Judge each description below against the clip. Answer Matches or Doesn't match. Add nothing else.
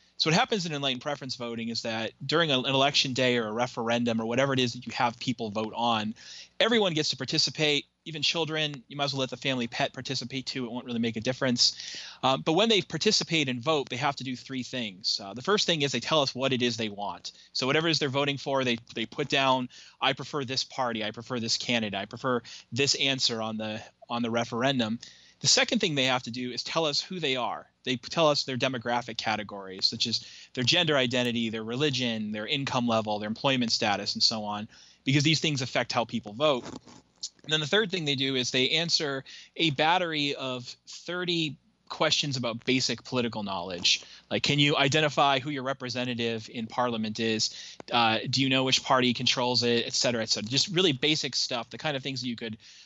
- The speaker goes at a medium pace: Doesn't match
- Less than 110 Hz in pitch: Doesn't match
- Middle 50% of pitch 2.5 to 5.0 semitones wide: Matches